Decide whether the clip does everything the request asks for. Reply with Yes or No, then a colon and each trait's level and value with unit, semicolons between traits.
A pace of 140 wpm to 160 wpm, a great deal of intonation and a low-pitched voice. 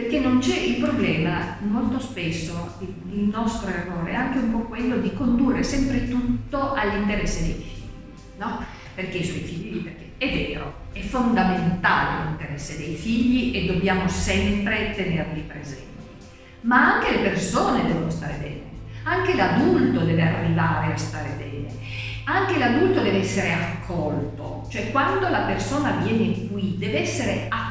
No: average, 145 wpm; wide, 8.6 semitones; medium, 180 Hz